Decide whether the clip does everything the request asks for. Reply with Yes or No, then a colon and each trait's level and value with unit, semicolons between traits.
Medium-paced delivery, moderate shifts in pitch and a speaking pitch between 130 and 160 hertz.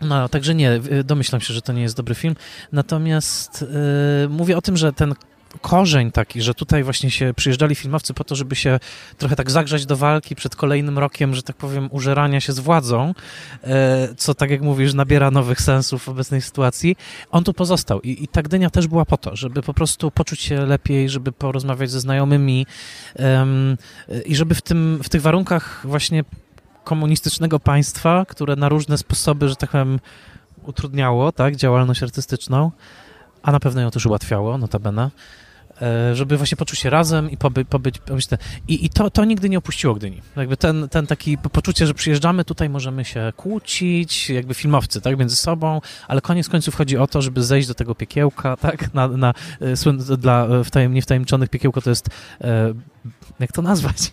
No: fast, 180 wpm; average, 3.0 semitones; medium, 140 Hz